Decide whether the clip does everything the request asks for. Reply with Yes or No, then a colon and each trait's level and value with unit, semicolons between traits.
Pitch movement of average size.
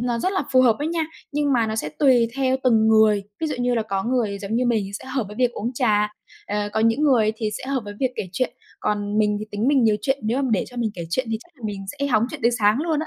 Yes: average, 3.6 semitones